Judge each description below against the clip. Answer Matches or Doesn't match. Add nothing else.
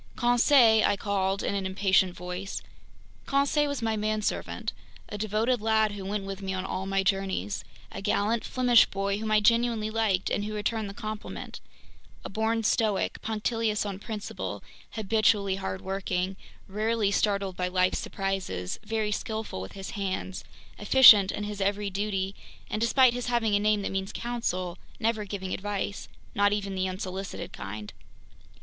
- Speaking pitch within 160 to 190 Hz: Doesn't match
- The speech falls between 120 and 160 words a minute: Matches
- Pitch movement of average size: Doesn't match